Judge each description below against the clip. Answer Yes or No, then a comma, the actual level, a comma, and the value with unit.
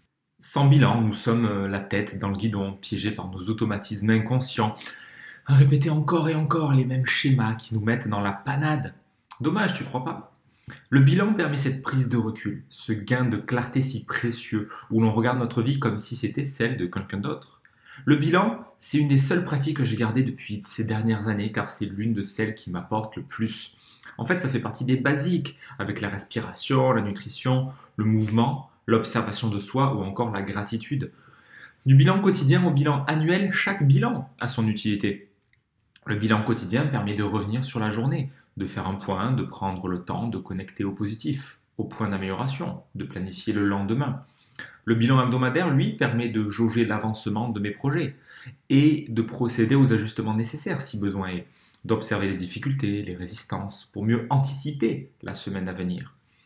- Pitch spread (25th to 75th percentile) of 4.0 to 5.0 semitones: Yes, average, 4.6 semitones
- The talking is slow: No, average, 185 wpm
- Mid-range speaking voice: No, low, 115 Hz